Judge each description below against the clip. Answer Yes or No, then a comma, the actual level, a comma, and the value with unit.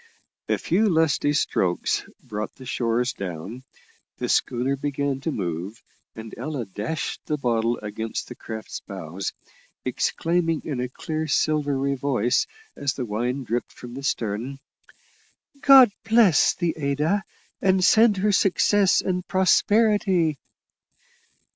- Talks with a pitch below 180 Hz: Yes, medium, 140 Hz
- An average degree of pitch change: No, wide, 6.5 semitones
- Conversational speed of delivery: No, slow, 125 wpm